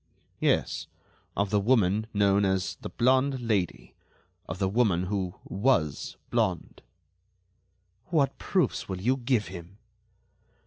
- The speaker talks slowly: Yes, slow, 120 wpm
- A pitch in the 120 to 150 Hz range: No, low, 100 Hz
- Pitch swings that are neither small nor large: Yes, average, 4.6 semitones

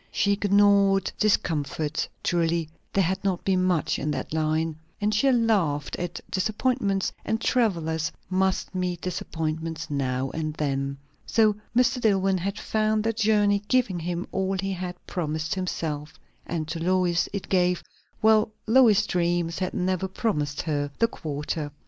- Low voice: No, medium, 185 Hz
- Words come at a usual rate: Yes, average, 145 wpm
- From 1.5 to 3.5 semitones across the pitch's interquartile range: No, average, 4.0 semitones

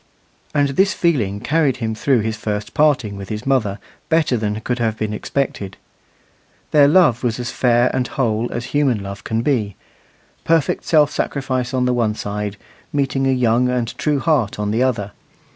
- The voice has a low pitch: Yes, low, 120 Hz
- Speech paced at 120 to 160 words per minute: No, average, 175 wpm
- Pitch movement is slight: No, average, 4.3 semitones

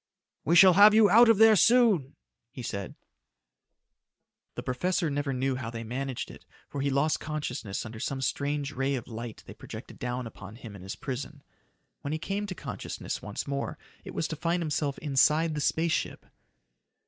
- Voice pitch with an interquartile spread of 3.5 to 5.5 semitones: Yes, average, 5.0 semitones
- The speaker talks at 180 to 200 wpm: Yes, average, 185 wpm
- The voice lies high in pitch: No, medium, 140 Hz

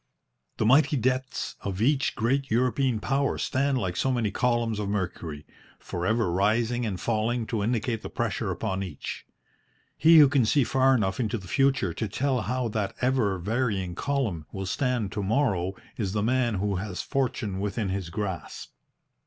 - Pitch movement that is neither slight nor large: Yes, average, 4.7 semitones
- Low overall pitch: Yes, low, 110 Hz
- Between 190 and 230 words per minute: No, average, 170 wpm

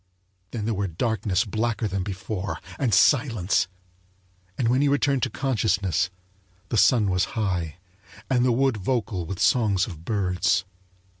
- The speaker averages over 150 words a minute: No, average, 145 wpm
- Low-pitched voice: Yes, low, 105 Hz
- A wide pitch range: No, average, 4.4 semitones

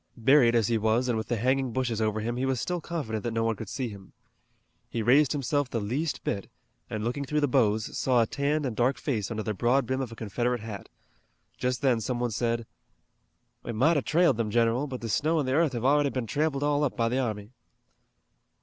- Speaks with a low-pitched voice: Yes, low, 120 Hz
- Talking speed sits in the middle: No, fast, 230 wpm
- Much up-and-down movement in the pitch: No, average, 3.5 semitones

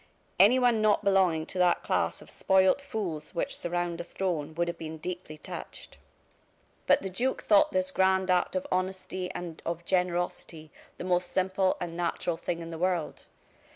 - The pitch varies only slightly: Yes, narrow, 2.0 semitones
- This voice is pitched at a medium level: Yes, medium, 180 Hz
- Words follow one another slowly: No, average, 170 wpm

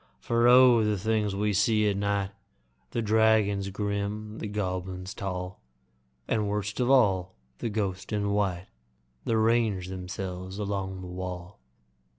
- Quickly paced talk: No, average, 140 wpm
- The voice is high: No, low, 100 Hz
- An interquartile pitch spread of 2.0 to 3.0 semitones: Yes, narrow, 2.4 semitones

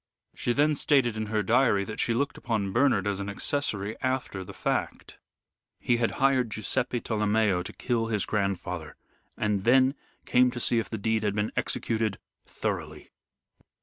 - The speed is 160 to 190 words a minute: Yes, average, 165 wpm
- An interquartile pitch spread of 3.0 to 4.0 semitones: Yes, average, 3.4 semitones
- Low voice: Yes, low, 110 Hz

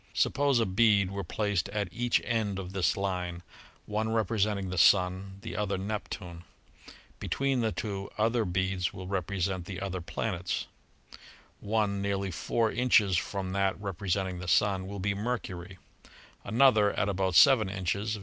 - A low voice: Yes, low, 100 Hz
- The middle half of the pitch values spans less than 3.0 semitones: Yes, narrow, 2.5 semitones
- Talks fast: No, average, 150 wpm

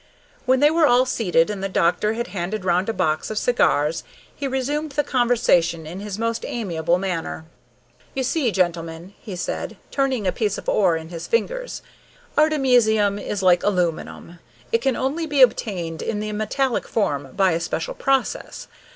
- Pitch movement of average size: No, wide, 6.7 semitones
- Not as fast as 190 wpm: Yes, average, 170 wpm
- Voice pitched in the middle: No, high, 210 Hz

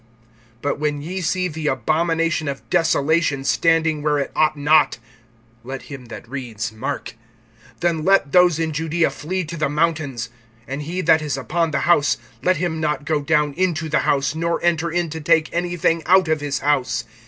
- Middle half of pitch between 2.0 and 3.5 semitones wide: Yes, average, 2.7 semitones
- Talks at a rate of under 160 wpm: No, average, 180 wpm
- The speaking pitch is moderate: Yes, medium, 155 Hz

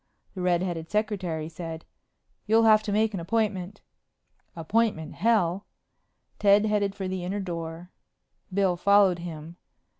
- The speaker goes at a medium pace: No, slow, 130 wpm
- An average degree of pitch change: Yes, average, 3.6 semitones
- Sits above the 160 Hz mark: Yes, high, 190 Hz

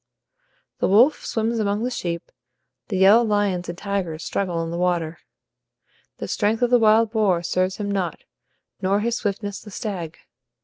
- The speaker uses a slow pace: No, average, 165 wpm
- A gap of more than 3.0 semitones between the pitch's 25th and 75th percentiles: Yes, average, 3.6 semitones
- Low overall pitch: No, high, 200 Hz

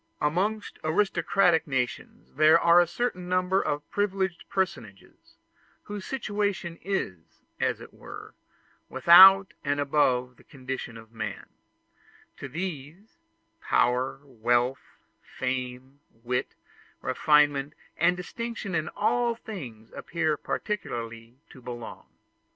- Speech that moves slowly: Yes, slow, 105 wpm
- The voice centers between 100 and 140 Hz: No, medium, 155 Hz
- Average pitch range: No, wide, 7.0 semitones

